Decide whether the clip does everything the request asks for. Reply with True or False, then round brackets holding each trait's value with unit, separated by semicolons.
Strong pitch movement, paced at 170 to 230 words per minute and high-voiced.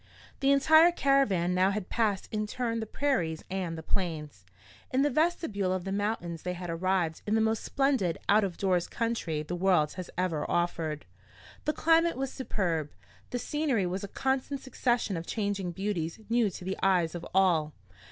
True (5.8 semitones; 180 wpm; 195 Hz)